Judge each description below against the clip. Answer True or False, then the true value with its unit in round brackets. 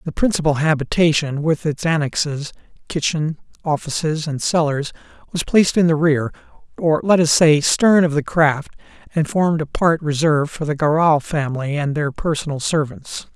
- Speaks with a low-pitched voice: False (155 Hz)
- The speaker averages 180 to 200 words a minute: False (145 wpm)